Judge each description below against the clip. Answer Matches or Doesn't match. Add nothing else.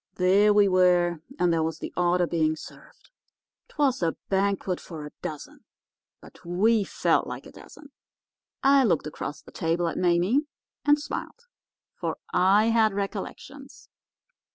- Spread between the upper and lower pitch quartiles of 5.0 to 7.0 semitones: Doesn't match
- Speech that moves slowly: Doesn't match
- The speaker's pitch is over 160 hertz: Matches